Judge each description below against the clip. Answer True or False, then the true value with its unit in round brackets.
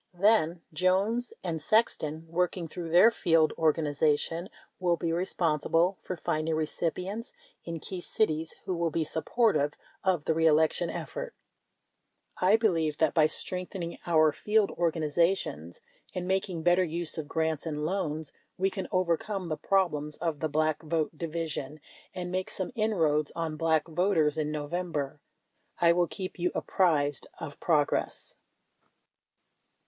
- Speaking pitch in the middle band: True (165 Hz)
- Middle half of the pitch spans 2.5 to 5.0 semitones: True (2.9 semitones)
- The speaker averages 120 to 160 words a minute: True (140 wpm)